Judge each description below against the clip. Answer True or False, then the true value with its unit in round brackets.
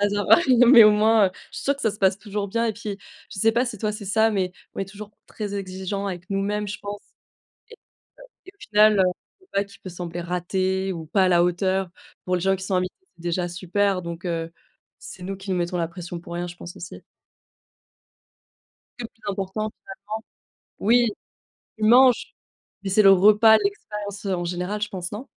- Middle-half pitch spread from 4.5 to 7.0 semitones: False (2.7 semitones)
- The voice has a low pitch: False (195 Hz)